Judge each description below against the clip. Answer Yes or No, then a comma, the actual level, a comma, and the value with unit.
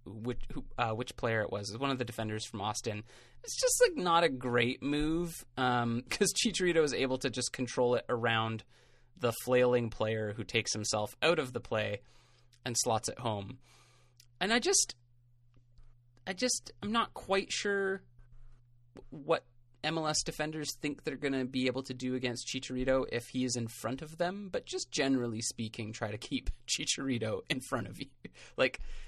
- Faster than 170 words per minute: Yes, average, 180 wpm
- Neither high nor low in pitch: No, low, 125 Hz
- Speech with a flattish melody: No, average, 3.7 semitones